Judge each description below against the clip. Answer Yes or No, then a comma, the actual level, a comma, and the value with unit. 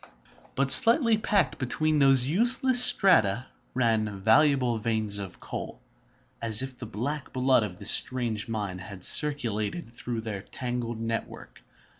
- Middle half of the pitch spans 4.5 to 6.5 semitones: Yes, average, 5.1 semitones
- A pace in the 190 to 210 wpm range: No, slow, 135 wpm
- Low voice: Yes, low, 120 Hz